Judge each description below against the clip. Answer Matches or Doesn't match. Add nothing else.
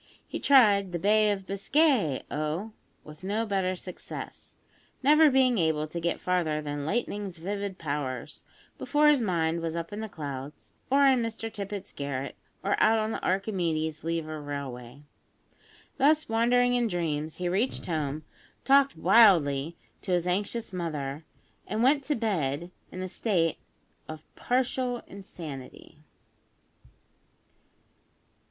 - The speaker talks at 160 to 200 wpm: Doesn't match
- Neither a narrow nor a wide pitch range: Doesn't match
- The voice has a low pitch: Doesn't match